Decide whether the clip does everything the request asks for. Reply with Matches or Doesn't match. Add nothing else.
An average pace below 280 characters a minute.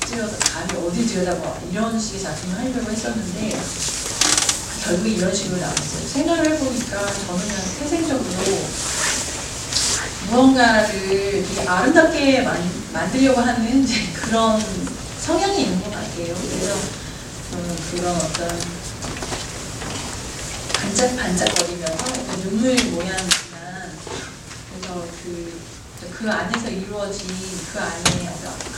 Matches